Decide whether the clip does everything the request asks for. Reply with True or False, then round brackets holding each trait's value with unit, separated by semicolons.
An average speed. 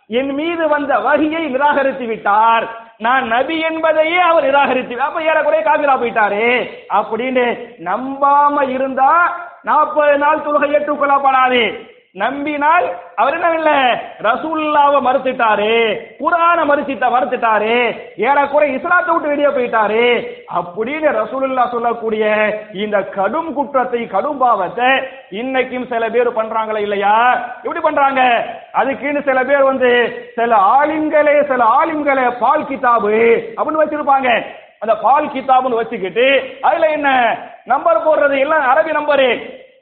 False (100 wpm)